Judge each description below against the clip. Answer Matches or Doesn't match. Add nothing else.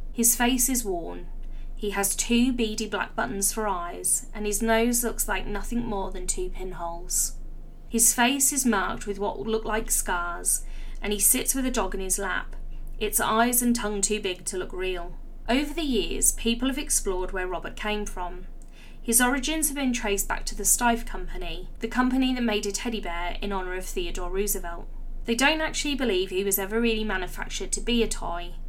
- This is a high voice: Matches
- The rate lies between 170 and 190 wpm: Doesn't match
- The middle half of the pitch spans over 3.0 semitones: Matches